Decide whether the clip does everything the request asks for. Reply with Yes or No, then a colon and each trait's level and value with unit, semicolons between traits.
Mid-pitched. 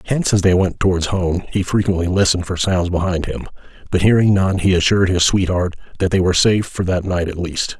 No: very low, 90 Hz